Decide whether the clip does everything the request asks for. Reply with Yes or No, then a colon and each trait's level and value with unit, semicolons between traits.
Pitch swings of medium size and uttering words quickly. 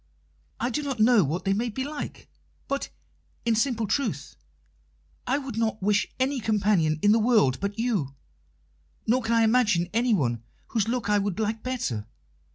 No: average, 3.7 semitones; average, 165 wpm